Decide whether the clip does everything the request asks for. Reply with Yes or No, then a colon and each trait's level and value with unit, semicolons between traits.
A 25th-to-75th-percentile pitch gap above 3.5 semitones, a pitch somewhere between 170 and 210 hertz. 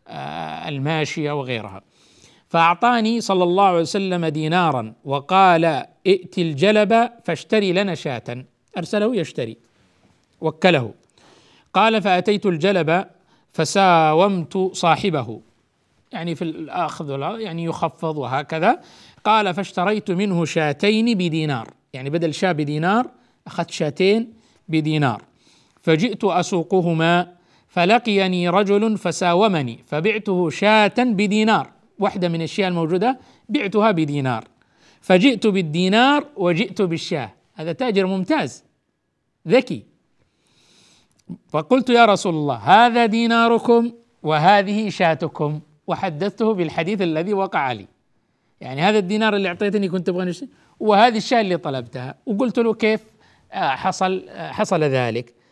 Yes: average, 4.7 semitones; medium, 185 Hz